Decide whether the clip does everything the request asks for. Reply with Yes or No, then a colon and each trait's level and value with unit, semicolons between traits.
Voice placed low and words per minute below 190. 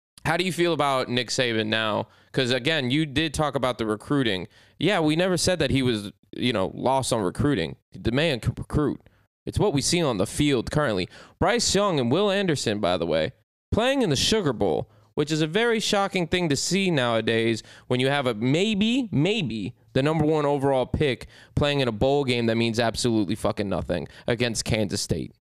No: low, 130 Hz; fast, 205 wpm